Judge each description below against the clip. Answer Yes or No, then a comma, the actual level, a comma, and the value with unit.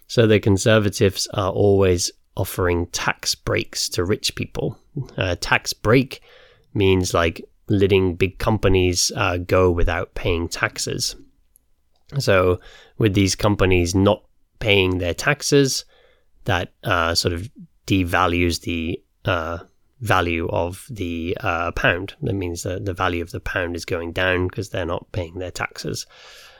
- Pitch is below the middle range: Yes, very low, 95 Hz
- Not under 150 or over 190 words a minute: No, average, 140 wpm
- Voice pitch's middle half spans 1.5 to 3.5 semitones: Yes, average, 2.8 semitones